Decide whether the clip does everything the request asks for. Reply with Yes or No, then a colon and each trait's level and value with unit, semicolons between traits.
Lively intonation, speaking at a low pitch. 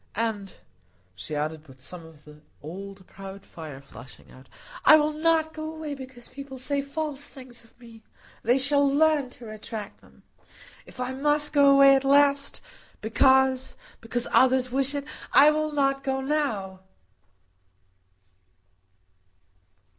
No: wide, 6.1 semitones; very high, 260 Hz